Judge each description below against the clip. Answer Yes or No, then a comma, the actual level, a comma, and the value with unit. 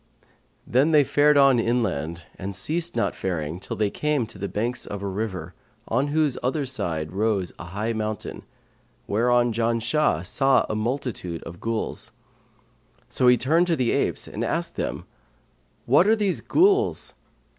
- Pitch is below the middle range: Yes, low, 115 Hz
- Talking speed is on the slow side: No, average, 155 wpm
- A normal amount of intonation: No, wide, 6.4 semitones